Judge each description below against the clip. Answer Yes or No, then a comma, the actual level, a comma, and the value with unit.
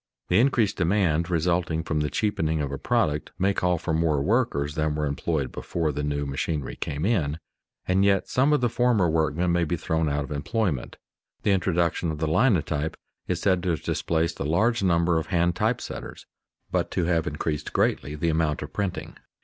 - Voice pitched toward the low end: Yes, very low, 80 Hz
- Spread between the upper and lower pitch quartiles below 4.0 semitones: Yes, average, 3.5 semitones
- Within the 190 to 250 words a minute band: Yes, average, 195 wpm